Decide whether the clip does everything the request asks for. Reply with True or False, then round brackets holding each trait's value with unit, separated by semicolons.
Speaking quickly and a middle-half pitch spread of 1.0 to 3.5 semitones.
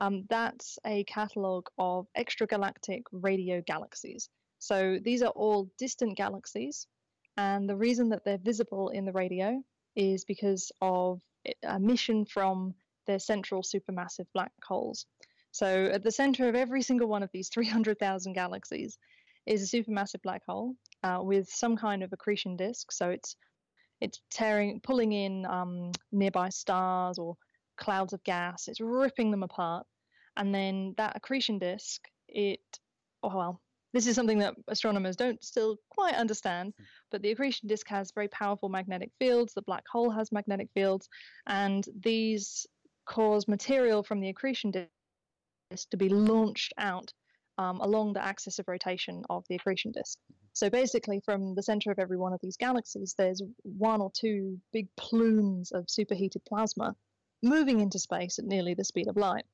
False (160 wpm; 2.8 semitones)